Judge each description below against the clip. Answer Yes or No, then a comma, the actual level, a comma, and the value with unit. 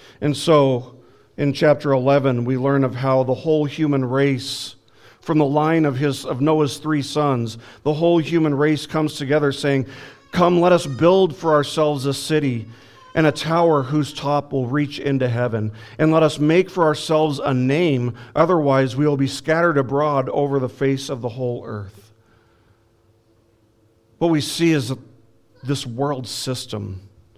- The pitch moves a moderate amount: Yes, average, 3.3 semitones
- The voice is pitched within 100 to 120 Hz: No, medium, 140 Hz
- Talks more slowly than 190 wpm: Yes, average, 160 wpm